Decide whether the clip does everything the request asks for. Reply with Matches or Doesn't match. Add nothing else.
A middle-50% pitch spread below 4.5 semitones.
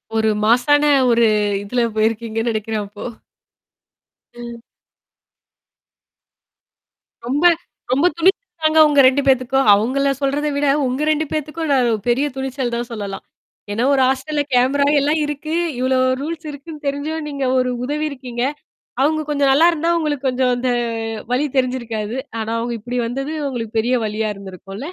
Matches